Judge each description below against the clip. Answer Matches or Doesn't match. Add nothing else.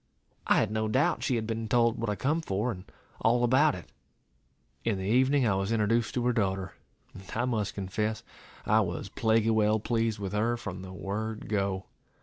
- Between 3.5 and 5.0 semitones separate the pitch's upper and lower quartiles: Doesn't match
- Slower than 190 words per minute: Doesn't match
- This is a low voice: Matches